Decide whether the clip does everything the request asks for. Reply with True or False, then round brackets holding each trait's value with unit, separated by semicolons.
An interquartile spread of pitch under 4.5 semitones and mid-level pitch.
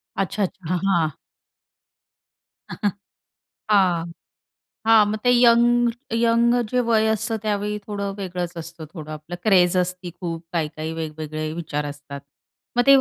False (5.1 semitones; 180 Hz)